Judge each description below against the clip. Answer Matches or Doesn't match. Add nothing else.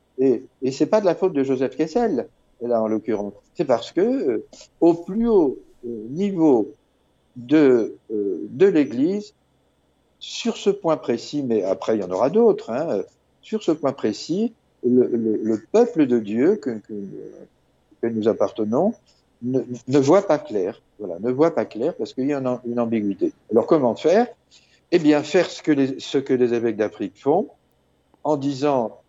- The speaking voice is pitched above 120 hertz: Matches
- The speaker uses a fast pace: Doesn't match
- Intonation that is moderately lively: Doesn't match